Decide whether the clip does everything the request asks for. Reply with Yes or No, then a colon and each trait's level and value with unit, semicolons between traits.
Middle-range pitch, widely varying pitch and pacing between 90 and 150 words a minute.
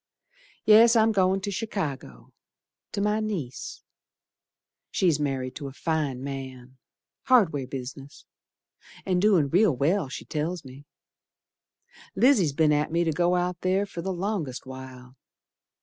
Yes: medium, 160 Hz; wide, 6.3 semitones; slow, 135 wpm